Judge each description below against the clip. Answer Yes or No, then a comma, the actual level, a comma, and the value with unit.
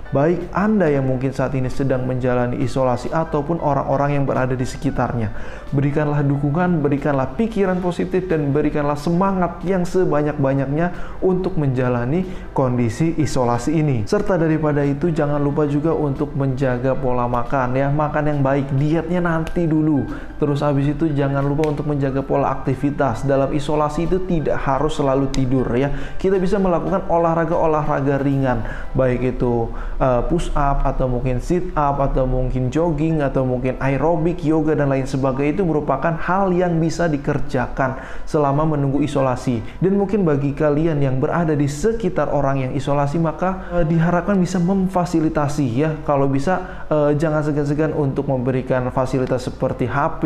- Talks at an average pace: No, fast, 150 wpm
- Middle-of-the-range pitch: Yes, medium, 145 Hz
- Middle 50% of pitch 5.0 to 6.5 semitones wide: No, average, 3.5 semitones